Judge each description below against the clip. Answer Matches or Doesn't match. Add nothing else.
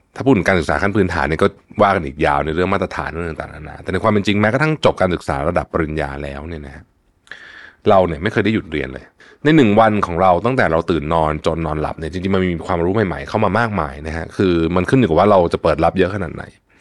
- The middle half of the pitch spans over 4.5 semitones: Doesn't match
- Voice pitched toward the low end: Matches